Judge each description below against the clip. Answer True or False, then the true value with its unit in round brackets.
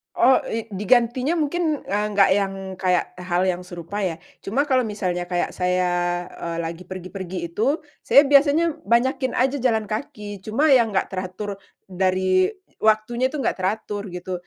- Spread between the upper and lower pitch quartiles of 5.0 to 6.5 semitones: True (5.6 semitones)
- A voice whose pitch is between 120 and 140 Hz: False (205 Hz)